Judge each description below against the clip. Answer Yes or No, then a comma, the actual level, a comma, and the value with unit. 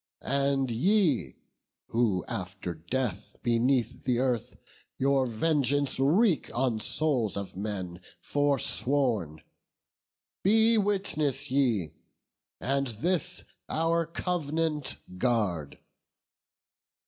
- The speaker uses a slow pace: Yes, slow, 85 wpm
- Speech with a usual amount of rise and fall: No, wide, 5.8 semitones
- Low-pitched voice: Yes, low, 130 Hz